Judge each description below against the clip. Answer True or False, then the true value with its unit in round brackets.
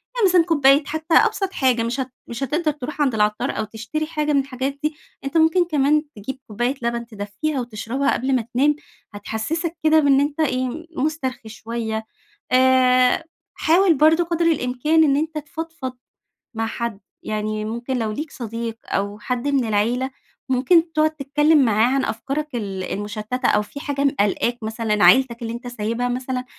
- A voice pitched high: True (260 Hz)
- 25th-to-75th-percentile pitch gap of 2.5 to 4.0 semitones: False (4.8 semitones)